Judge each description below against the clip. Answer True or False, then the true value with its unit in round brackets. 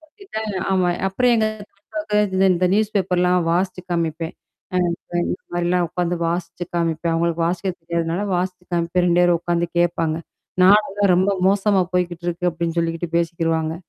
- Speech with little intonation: True (2.0 semitones)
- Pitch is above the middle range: False (175 Hz)